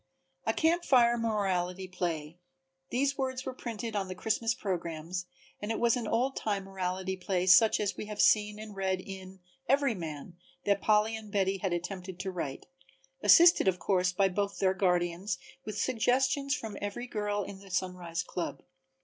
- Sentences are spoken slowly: No, average, 175 wpm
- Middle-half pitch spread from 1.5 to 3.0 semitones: No, average, 3.5 semitones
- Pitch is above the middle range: Yes, high, 195 Hz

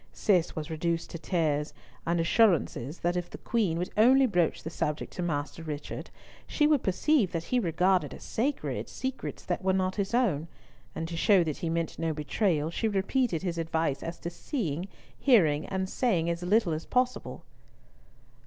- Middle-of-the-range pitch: Yes, medium, 175 Hz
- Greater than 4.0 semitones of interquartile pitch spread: Yes, average, 4.5 semitones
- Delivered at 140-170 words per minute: No, average, 180 wpm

